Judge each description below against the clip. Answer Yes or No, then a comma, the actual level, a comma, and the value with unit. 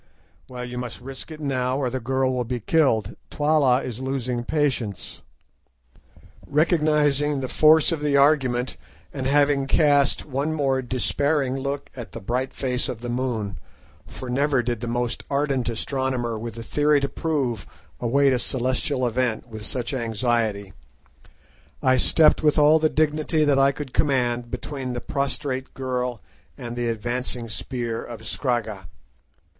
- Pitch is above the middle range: No, low, 130 Hz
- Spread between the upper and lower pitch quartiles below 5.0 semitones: Yes, average, 2.9 semitones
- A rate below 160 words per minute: Yes, average, 150 wpm